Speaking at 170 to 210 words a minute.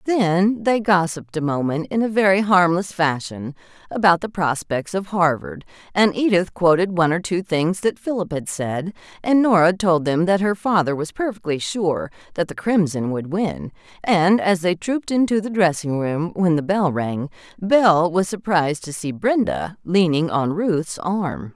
Yes: average, 175 wpm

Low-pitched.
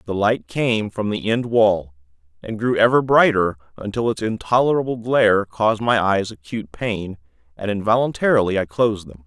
Yes: low, 105 Hz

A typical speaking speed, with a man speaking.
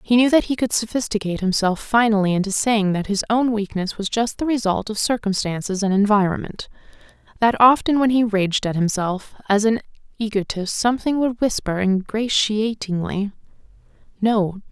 No: average, 150 wpm; female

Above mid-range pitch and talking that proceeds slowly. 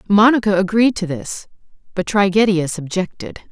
Yes: high, 195 Hz; slow, 120 wpm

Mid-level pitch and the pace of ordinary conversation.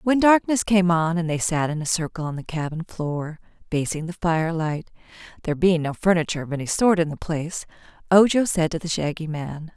Yes: medium, 170 Hz; average, 190 wpm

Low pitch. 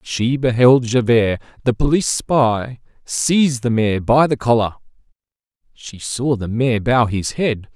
Yes: low, 120 Hz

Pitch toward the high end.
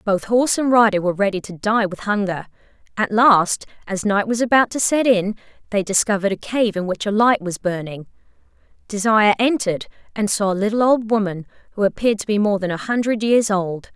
Yes: high, 205 Hz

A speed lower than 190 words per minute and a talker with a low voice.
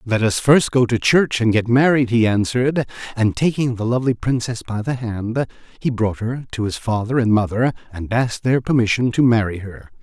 No: fast, 205 wpm; low, 120 Hz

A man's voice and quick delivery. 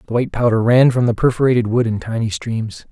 Yes: male; fast, 225 wpm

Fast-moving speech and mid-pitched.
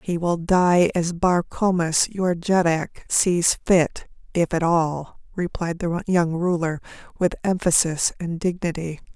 No: average, 140 wpm; medium, 170 Hz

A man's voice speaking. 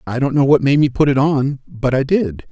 Yes: male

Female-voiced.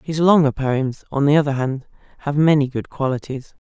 Yes: female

